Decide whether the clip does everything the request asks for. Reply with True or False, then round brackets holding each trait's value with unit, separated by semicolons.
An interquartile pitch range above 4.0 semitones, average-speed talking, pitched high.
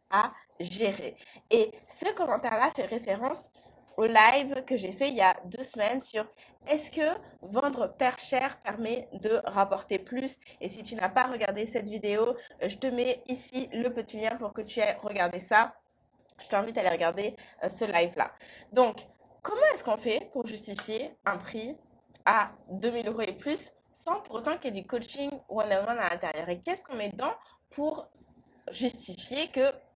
True (4.4 semitones; 175 wpm; 235 Hz)